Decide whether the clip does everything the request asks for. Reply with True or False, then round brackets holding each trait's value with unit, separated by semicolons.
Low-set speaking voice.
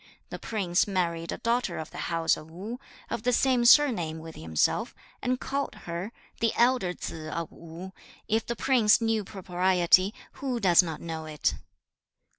False (185 Hz)